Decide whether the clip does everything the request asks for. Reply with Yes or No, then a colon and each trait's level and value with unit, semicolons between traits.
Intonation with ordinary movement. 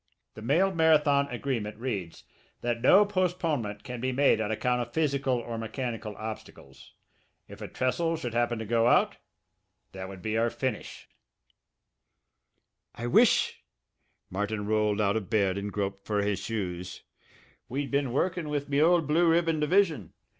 No: wide, 5.7 semitones